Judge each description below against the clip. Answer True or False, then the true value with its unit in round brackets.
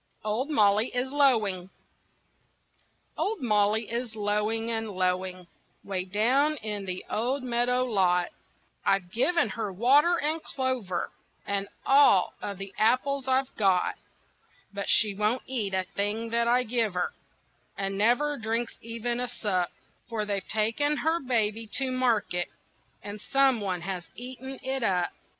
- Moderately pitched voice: False (225 Hz)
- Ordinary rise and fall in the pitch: True (4.2 semitones)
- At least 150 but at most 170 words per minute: False (140 wpm)